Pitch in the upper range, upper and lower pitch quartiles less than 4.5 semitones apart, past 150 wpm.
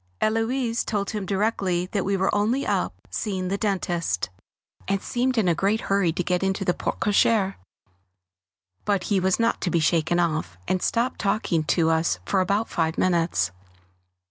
Yes: high, 195 Hz; average, 3.4 semitones; average, 170 wpm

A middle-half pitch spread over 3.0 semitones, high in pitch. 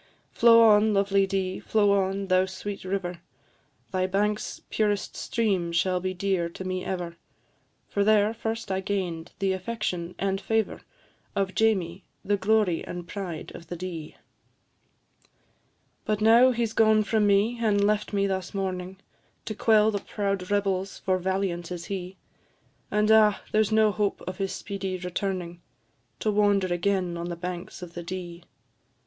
No: narrow, 2.4 semitones; high, 195 Hz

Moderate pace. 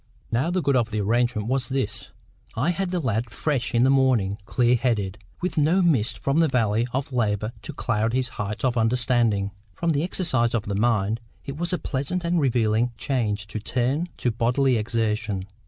Yes: average, 190 wpm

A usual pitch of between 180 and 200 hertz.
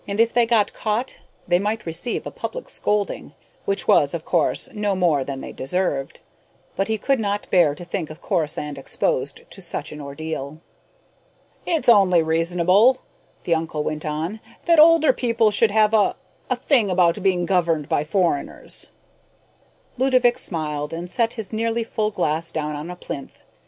Yes: medium, 185 Hz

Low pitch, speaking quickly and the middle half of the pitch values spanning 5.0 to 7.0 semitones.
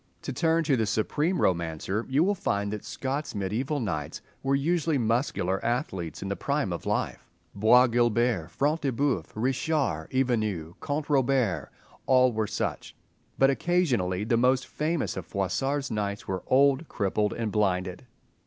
No: low, 120 Hz; average, 155 wpm; wide, 5.6 semitones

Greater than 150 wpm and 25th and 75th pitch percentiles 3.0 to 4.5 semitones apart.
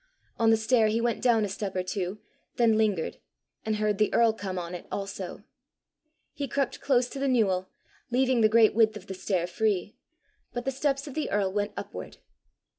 Yes: average, 195 wpm; average, 3.7 semitones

